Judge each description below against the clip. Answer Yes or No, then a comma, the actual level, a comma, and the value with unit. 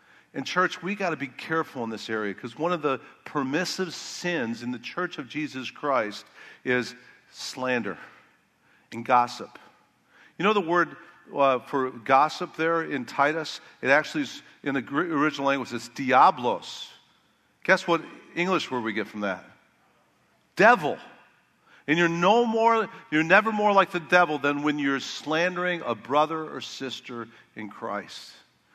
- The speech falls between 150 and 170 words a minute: Yes, average, 155 wpm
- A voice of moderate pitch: Yes, medium, 150 Hz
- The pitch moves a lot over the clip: Yes, wide, 6.2 semitones